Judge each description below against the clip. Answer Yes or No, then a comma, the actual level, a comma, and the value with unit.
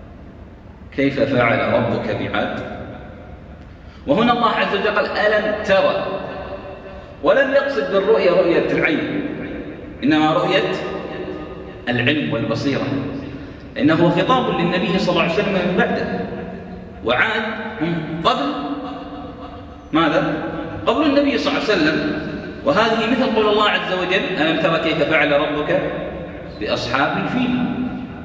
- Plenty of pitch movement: Yes, wide, 8.6 semitones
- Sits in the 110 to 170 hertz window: No, high, 190 Hz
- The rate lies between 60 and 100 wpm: No, average, 110 wpm